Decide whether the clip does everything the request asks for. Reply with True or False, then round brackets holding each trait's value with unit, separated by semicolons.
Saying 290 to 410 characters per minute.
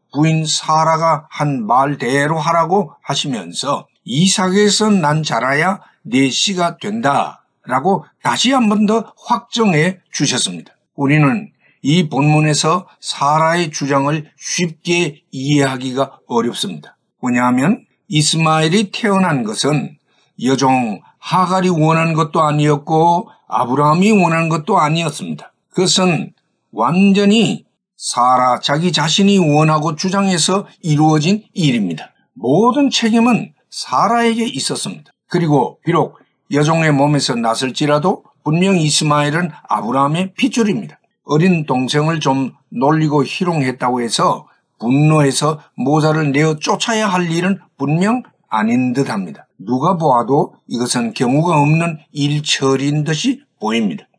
False (275 characters per minute)